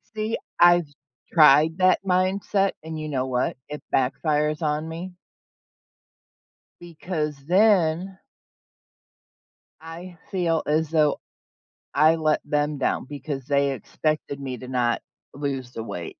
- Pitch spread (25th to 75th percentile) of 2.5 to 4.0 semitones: Yes, average, 3.6 semitones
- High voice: No, medium, 155 Hz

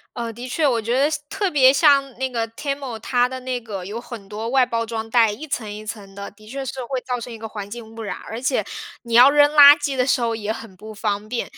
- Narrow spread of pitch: No, average, 3.3 semitones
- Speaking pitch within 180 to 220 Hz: No, high, 235 Hz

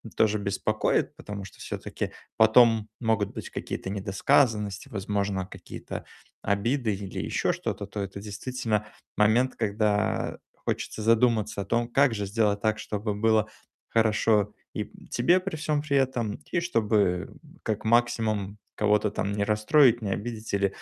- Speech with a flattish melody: Yes, narrow, 2.3 semitones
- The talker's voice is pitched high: No, low, 110 Hz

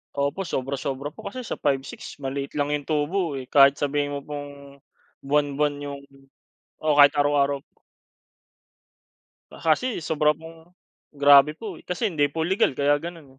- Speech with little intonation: Yes, narrow, 2.2 semitones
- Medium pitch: Yes, medium, 145 Hz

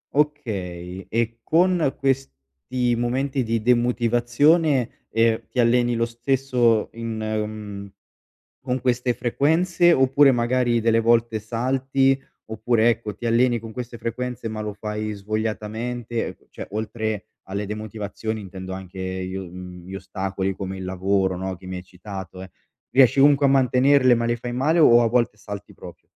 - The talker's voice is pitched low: Yes, low, 115 Hz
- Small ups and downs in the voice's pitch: No, average, 3.7 semitones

